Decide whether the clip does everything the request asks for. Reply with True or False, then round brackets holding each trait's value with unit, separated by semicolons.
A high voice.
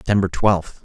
False (95 Hz)